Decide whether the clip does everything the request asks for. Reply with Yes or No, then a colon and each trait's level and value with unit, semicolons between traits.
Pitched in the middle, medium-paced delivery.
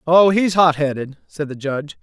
No: medium, 160 Hz; fast, 210 wpm